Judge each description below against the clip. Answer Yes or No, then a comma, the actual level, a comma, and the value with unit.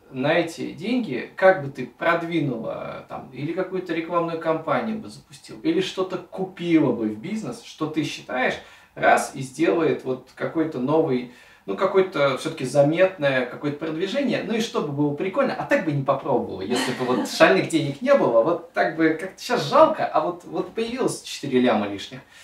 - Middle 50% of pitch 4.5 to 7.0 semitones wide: Yes, average, 5.2 semitones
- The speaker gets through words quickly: Yes, fast, 175 wpm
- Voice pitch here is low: No, medium, 165 Hz